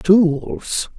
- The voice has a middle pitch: Yes, medium, 165 Hz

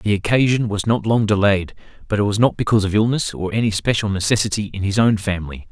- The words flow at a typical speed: No, fast, 210 wpm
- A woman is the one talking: No, male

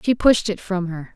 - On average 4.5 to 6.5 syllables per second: Yes, 4.8 syllables/s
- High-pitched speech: Yes, high, 195 Hz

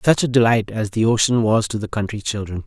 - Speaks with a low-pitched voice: Yes, low, 110 Hz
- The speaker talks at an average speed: No, fast, 250 wpm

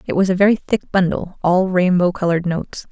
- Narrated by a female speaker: Yes, female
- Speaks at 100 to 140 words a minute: No, fast, 205 wpm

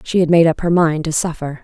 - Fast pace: Yes, fast, 295 wpm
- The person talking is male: No, female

